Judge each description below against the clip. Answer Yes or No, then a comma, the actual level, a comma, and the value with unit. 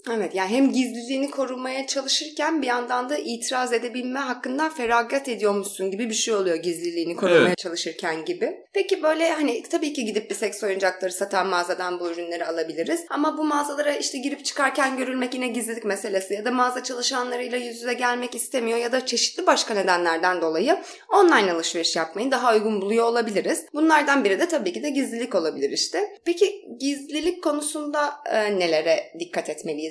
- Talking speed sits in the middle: No, fast, 165 wpm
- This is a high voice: Yes, very high, 250 Hz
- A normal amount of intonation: No, wide, 6.7 semitones